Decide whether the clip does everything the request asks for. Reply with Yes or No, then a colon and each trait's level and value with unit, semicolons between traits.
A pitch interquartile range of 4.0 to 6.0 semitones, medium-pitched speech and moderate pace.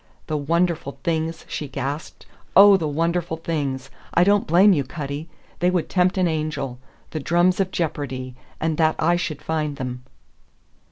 No: average, 3.3 semitones; medium, 160 Hz; average, 160 wpm